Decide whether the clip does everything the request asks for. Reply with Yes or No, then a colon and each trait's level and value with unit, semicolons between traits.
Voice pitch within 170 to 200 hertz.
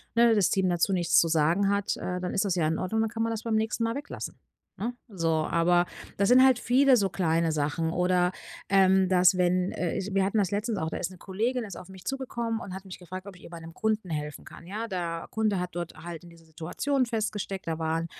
Yes: medium, 185 Hz